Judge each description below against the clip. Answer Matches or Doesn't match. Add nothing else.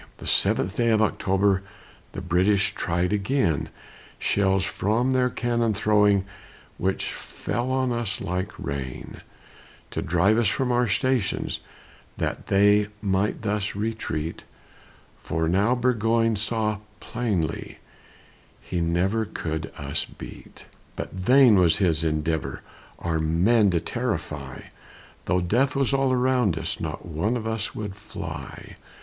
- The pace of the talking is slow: Matches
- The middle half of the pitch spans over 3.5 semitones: Matches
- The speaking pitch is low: Matches